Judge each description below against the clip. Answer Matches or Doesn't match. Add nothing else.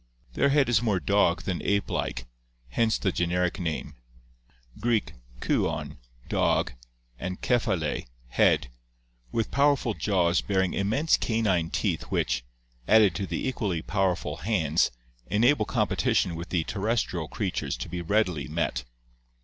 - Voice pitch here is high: Doesn't match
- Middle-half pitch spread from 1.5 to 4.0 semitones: Doesn't match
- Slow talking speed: Matches